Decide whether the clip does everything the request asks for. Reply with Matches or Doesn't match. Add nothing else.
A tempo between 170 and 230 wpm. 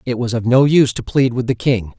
Doesn't match